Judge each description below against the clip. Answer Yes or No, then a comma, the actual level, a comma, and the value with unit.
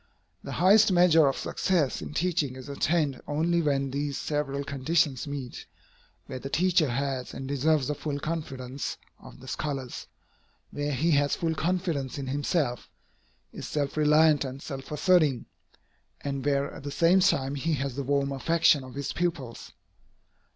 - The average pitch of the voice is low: No, medium, 145 Hz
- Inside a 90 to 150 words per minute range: No, average, 160 wpm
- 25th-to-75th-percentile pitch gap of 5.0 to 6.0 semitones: No, average, 3.0 semitones